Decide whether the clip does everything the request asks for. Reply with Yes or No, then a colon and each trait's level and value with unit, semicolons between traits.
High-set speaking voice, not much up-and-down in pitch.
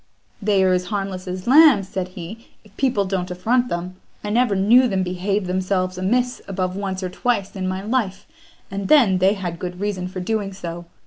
Yes: high, 195 Hz; narrow, 2.3 semitones